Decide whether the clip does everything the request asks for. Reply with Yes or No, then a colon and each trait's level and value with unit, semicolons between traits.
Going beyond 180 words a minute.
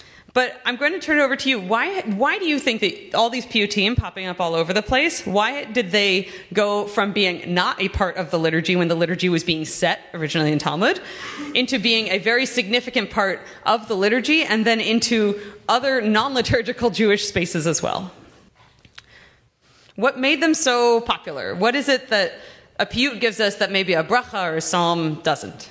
Yes: average, 200 wpm